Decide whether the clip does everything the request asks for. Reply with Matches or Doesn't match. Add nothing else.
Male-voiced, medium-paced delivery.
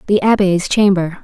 Doesn't match